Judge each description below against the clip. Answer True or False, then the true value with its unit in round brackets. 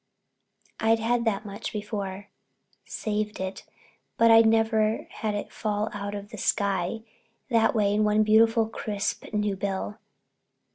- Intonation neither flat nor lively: False (1.6 semitones)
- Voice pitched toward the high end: True (210 Hz)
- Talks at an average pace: False (130 wpm)